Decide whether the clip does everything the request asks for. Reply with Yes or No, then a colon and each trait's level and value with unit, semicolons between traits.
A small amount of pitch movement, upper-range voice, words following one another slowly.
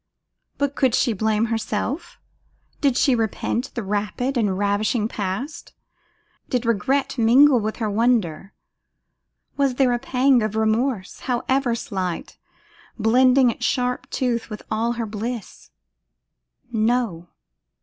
No: average, 3.0 semitones; high, 235 Hz; slow, 120 wpm